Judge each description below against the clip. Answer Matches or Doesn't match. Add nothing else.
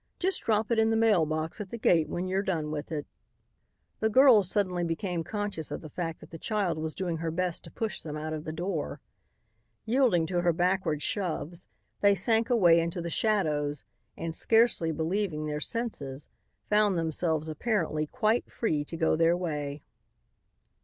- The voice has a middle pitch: Matches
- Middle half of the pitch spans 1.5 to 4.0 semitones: Doesn't match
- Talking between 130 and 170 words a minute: Doesn't match